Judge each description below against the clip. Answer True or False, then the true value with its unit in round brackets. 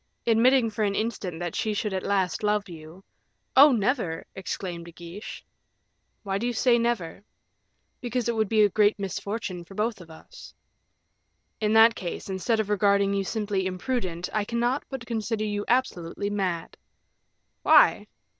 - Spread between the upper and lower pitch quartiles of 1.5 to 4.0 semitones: True (3.4 semitones)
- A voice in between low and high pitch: False (205 Hz)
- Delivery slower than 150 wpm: False (165 wpm)